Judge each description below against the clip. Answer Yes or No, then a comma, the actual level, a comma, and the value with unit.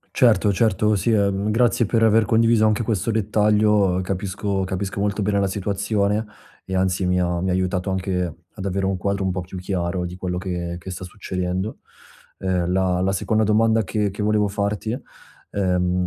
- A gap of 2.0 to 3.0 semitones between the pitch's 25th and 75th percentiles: Yes, narrow, 2.4 semitones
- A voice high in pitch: No, low, 100 Hz